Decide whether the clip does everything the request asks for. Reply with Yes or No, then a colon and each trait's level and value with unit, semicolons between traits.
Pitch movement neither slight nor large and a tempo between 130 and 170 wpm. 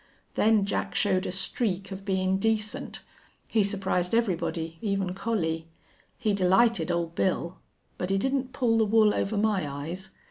Yes: average, 3.4 semitones; average, 150 wpm